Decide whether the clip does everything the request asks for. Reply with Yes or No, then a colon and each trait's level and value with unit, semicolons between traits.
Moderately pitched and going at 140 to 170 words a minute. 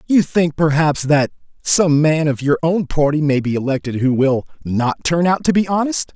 No: medium, 155 Hz; fast, 205 wpm